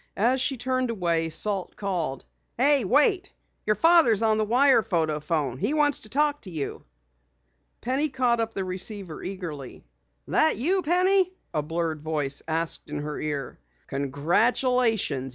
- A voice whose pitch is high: Yes, high, 205 Hz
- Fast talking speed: No, average, 150 wpm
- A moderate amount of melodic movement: No, wide, 8.6 semitones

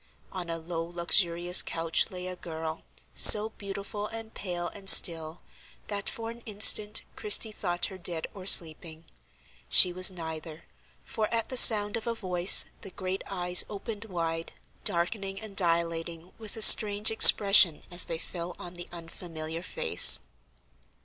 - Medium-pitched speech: Yes, medium, 180 Hz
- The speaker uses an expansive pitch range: No, average, 3.6 semitones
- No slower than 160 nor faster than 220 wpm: No, average, 150 wpm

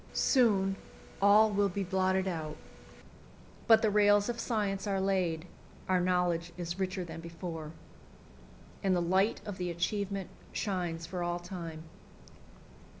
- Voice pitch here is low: No, medium, 185 Hz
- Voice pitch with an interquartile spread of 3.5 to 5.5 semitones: No, narrow, 2.6 semitones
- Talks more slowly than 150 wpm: Yes, slow, 135 wpm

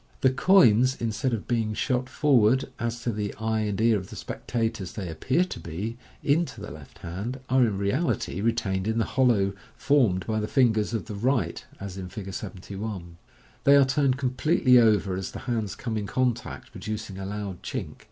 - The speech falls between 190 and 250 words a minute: Yes, average, 195 wpm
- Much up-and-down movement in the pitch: No, average, 4.3 semitones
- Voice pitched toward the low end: Yes, low, 110 Hz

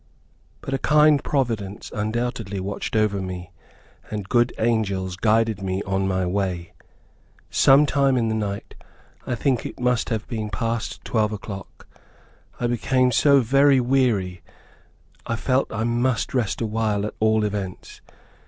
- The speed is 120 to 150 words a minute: Yes, average, 145 wpm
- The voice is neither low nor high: No, low, 110 Hz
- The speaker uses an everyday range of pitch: Yes, average, 3.8 semitones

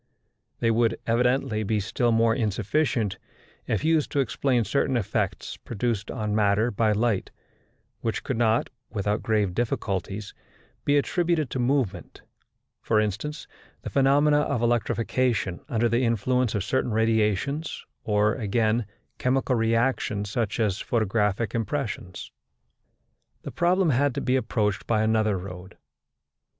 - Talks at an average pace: No, slow, 130 wpm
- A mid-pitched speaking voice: No, low, 115 Hz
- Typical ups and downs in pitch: Yes, average, 3.4 semitones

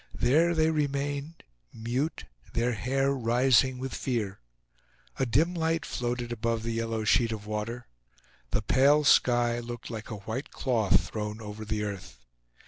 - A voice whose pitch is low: Yes, low, 120 Hz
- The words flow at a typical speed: Yes, average, 145 wpm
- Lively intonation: No, average, 3.7 semitones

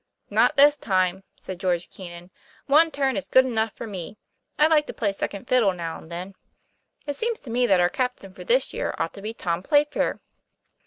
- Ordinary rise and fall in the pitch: No, wide, 7.2 semitones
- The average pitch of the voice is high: Yes, high, 220 Hz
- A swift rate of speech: Yes, fast, 210 wpm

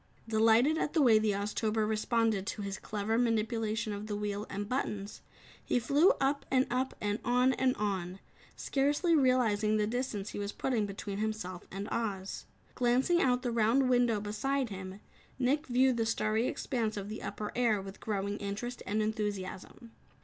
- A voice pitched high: Yes, high, 220 Hz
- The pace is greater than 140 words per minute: Yes, average, 170 wpm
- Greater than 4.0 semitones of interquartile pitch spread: No, average, 3.4 semitones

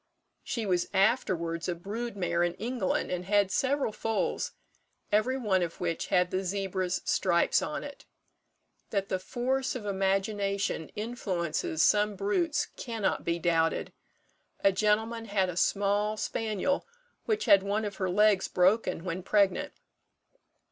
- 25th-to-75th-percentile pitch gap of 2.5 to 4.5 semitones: Yes, average, 3.1 semitones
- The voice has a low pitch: No, high, 200 Hz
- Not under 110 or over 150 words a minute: Yes, average, 140 wpm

